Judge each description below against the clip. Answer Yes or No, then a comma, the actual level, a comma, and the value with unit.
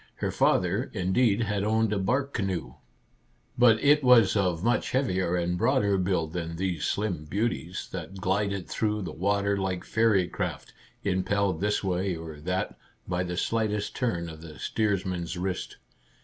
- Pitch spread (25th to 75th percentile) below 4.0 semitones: Yes, average, 3.1 semitones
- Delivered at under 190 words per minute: Yes, average, 155 wpm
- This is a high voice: No, very low, 95 Hz